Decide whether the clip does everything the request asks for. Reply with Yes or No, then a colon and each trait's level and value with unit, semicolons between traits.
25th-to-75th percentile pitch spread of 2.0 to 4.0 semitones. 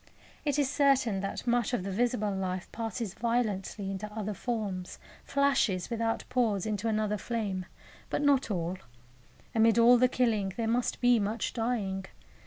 Yes: average, 3.7 semitones